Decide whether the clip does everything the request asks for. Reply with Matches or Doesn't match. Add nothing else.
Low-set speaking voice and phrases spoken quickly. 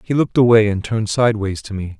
Matches